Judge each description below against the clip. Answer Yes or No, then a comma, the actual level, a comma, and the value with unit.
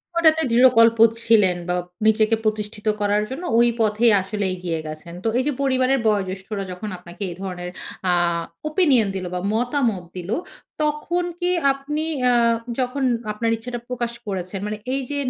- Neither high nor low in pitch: No, high, 220 Hz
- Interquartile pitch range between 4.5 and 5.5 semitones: Yes, average, 4.8 semitones